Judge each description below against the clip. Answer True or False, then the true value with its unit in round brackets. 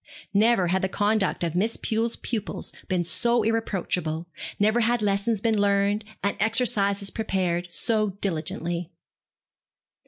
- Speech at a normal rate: False (125 wpm)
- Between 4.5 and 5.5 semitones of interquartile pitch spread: False (3.4 semitones)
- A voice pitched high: True (200 Hz)